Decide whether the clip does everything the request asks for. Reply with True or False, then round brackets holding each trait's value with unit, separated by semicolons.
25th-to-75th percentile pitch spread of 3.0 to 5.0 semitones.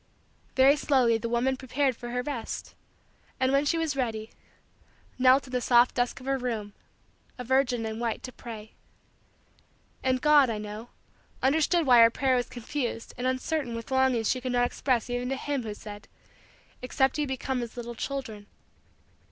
False (2.4 semitones)